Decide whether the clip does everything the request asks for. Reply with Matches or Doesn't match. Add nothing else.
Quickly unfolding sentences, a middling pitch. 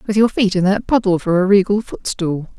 Doesn't match